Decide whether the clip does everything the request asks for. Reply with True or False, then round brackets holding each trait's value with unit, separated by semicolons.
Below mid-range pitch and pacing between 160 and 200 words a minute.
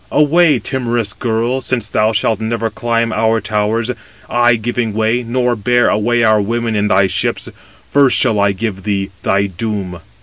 True (115 Hz; 165 wpm)